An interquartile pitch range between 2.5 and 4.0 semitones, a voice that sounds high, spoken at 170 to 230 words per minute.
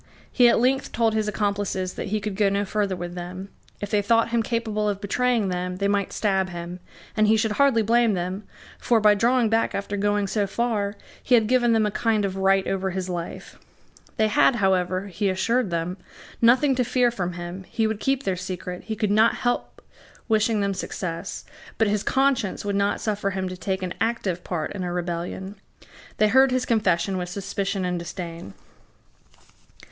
Yes: average, 3.2 semitones; high, 205 Hz; average, 195 wpm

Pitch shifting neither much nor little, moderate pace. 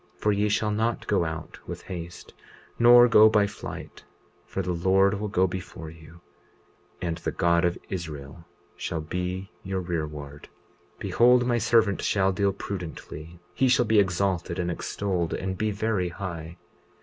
Yes: average, 3.5 semitones; average, 160 wpm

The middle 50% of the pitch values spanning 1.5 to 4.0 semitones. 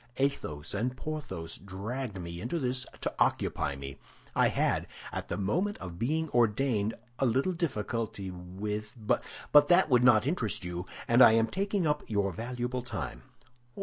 No: wide, 5.5 semitones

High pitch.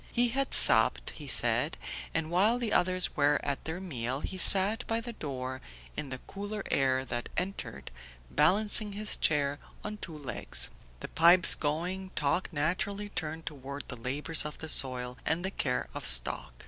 No: medium, 160 Hz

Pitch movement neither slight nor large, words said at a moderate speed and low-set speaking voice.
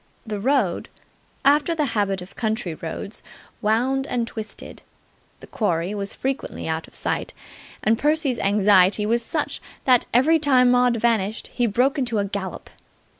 No: average, 4.3 semitones; average, 150 wpm; high, 230 Hz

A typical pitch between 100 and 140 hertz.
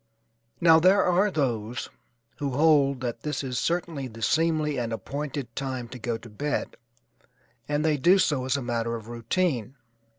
Yes: low, 135 Hz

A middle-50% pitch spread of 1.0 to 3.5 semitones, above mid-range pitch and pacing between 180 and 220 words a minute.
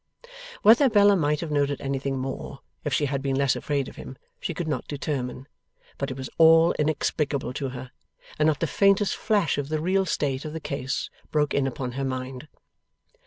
No: average, 3.2 semitones; medium, 145 Hz; average, 195 wpm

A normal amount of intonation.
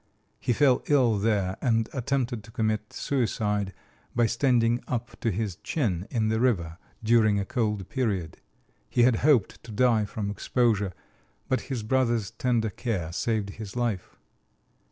Yes: average, 3.1 semitones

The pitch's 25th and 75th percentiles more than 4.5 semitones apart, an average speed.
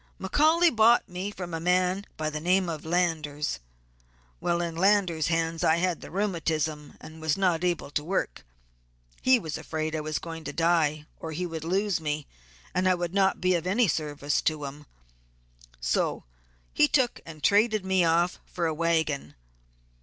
No: average, 3.0 semitones; average, 175 wpm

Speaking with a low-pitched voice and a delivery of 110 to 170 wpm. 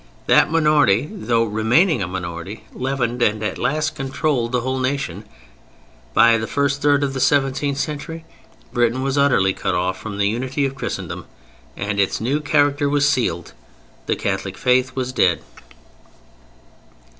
Yes: low, 130 Hz; average, 150 wpm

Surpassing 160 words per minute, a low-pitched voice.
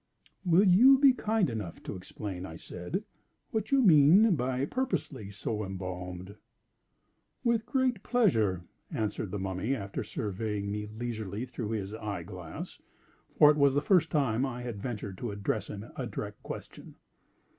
No: average, 150 wpm; low, 115 Hz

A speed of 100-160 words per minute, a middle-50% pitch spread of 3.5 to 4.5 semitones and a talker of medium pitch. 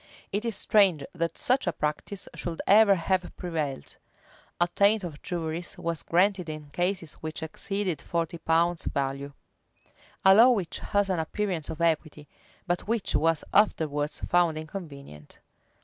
Yes: average, 150 wpm; average, 3.9 semitones; medium, 170 Hz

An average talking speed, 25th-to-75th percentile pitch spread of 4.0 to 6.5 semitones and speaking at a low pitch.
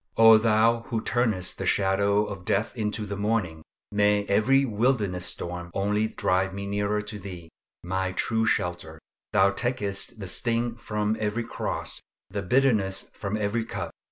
No: average, 150 wpm; average, 2.7 semitones; low, 105 Hz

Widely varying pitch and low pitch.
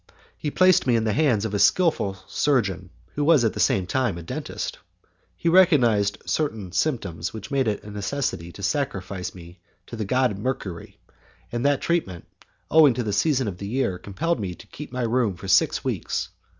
Yes: wide, 6.3 semitones; low, 110 Hz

